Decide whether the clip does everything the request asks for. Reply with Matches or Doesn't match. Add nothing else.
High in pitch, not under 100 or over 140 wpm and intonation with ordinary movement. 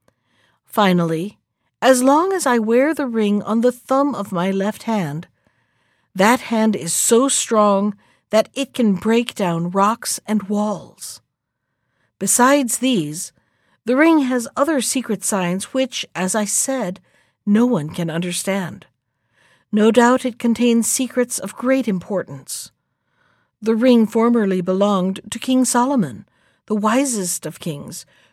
Matches